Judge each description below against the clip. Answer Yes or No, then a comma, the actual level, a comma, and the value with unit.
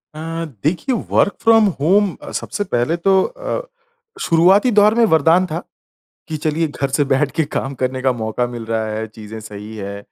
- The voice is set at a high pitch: No, medium, 155 Hz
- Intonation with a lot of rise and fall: Yes, wide, 8.1 semitones